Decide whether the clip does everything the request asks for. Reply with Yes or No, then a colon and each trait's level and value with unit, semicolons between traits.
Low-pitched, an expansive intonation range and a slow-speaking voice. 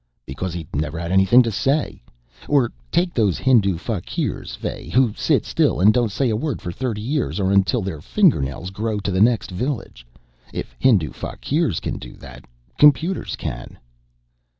No: low, 105 Hz; wide, 6.1 semitones; average, 170 wpm